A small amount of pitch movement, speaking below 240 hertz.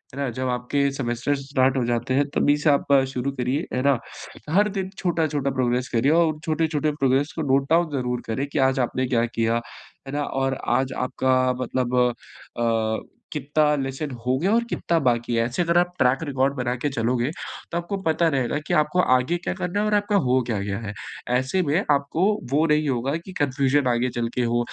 No: average, 3.7 semitones; low, 135 Hz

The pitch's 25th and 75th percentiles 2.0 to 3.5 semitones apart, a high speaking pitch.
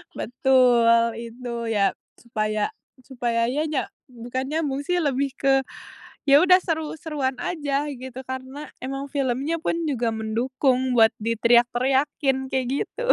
Yes: average, 3.0 semitones; very high, 260 Hz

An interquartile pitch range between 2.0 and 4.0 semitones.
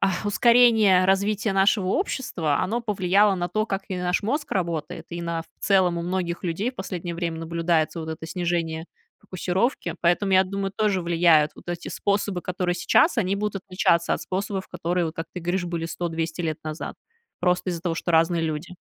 Yes: average, 2.7 semitones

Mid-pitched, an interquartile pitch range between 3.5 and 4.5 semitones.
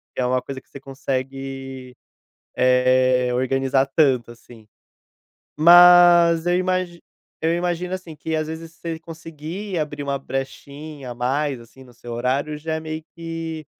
Yes: medium, 145 Hz; average, 4.1 semitones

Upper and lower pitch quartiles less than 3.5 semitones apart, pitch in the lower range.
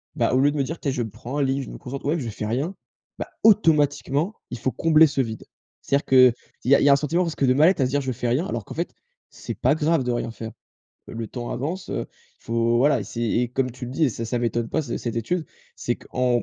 No: average, 3.8 semitones; low, 130 Hz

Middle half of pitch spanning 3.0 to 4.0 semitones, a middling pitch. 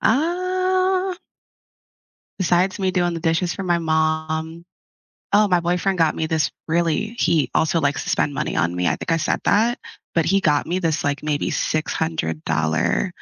Yes: average, 3.6 semitones; medium, 165 Hz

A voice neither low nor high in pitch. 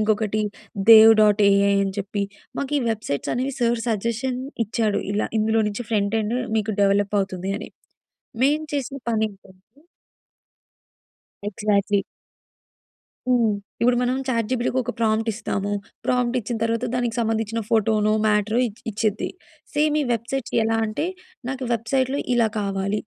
No: high, 220 Hz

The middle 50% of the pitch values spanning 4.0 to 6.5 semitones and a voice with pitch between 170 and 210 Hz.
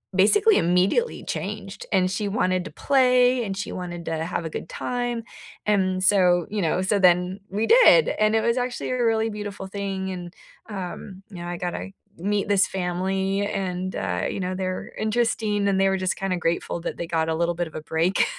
No: average, 3.0 semitones; high, 190 Hz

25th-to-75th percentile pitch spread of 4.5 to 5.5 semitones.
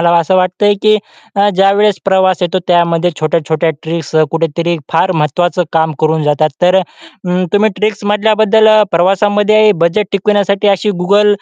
No: average, 3.5 semitones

